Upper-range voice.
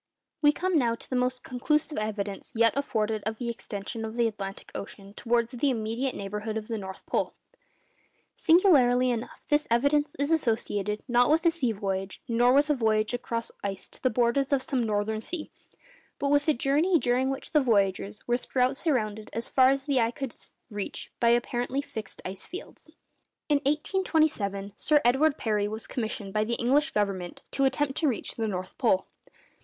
Yes: high, 240 Hz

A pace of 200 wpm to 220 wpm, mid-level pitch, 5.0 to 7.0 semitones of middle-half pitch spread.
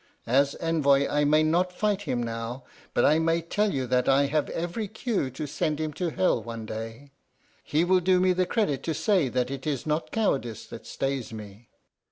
Yes: fast, 205 wpm; medium, 150 Hz; wide, 5.4 semitones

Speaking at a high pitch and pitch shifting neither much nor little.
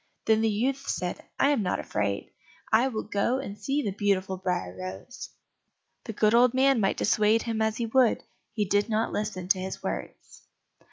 Yes: high, 215 Hz; average, 3.7 semitones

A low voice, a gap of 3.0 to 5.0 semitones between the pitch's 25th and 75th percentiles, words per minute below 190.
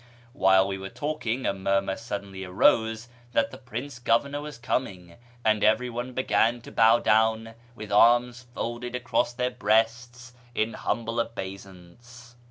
Yes: low, 115 Hz; average, 3.3 semitones; average, 140 wpm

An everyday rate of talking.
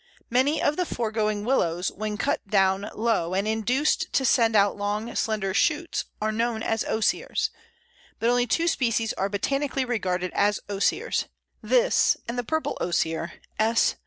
Yes: average, 155 wpm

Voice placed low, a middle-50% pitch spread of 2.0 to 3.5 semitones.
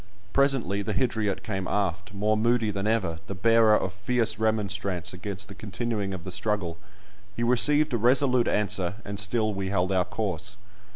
Yes: low, 105 Hz; average, 3.0 semitones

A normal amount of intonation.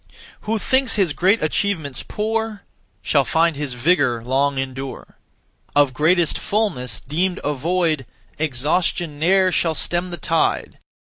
Yes: average, 4.7 semitones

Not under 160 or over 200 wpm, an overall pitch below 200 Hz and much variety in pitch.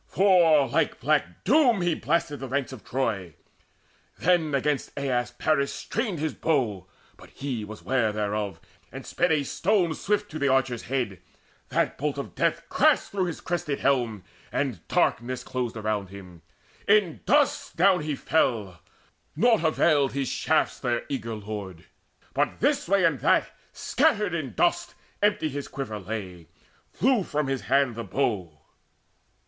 No: average, 150 wpm; low, 135 Hz; wide, 7.3 semitones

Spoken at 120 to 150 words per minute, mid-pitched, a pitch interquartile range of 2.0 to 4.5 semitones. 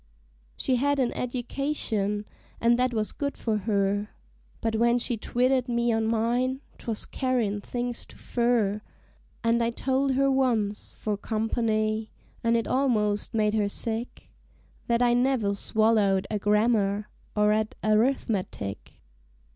No: average, 140 wpm; high, 230 Hz; average, 2.7 semitones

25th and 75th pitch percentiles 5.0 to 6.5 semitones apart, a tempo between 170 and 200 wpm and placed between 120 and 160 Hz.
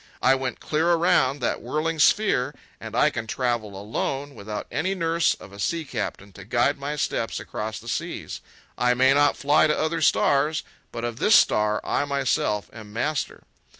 Yes: wide, 5.4 semitones; average, 180 wpm; low, 135 Hz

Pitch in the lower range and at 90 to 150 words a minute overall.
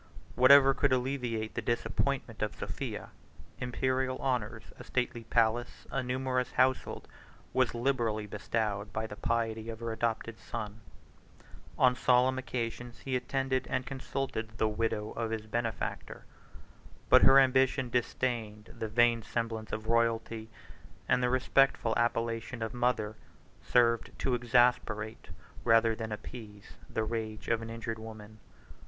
Yes: low, 115 Hz; slow, 135 wpm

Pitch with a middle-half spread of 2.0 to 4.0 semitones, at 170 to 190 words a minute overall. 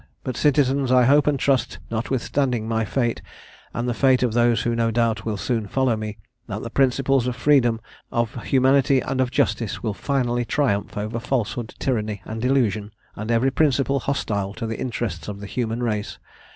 Yes: average, 3.1 semitones; average, 180 wpm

